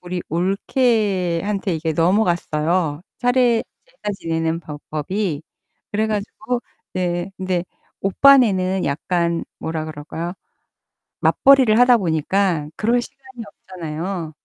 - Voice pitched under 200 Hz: Yes, medium, 185 Hz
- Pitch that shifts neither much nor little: Yes, average, 4.7 semitones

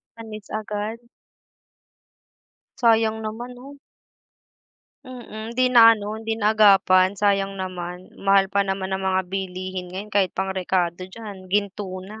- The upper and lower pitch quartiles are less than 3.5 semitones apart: Yes, narrow, 2.6 semitones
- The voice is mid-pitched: No, high, 200 Hz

